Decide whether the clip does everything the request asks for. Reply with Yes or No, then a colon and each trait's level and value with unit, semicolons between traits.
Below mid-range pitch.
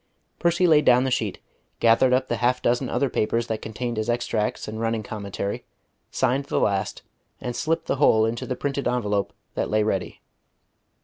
Yes: low, 120 Hz